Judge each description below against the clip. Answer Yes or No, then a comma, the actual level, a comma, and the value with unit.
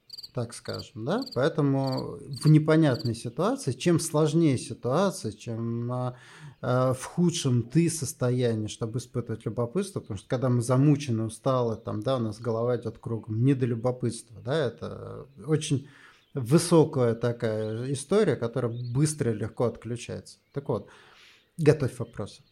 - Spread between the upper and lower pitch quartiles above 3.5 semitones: Yes, average, 4.0 semitones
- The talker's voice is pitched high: No, low, 125 Hz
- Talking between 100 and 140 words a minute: Yes, average, 130 wpm